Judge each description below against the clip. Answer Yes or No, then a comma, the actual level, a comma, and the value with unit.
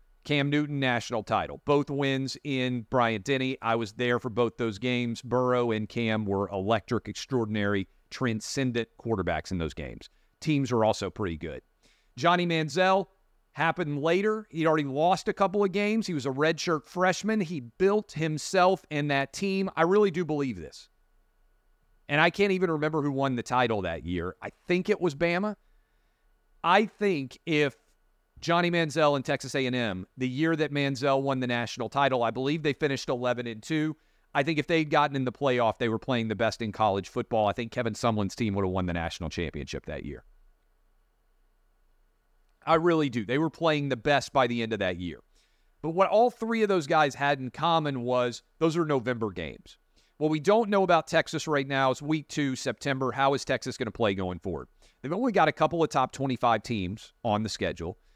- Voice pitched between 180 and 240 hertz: No, low, 135 Hz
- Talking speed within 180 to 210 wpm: Yes, average, 190 wpm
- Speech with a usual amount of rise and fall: No, wide, 5.9 semitones